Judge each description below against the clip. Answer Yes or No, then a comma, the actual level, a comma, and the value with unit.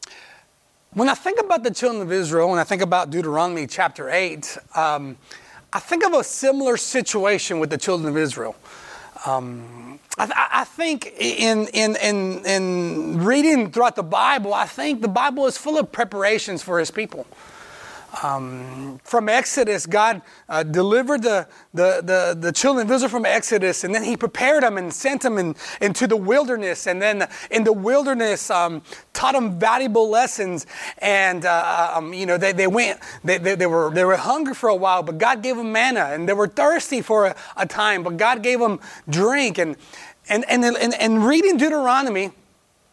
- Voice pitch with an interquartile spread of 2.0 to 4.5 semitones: No, wide, 5.5 semitones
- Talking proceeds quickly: No, average, 185 wpm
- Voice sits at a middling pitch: No, high, 210 Hz